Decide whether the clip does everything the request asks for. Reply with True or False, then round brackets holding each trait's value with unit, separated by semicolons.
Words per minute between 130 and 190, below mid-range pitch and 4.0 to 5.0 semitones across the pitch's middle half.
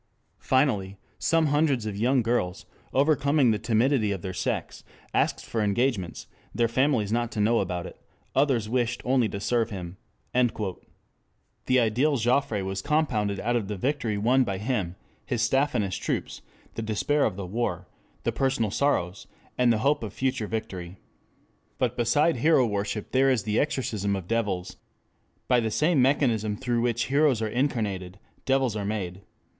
True (165 wpm; 115 Hz; 4.4 semitones)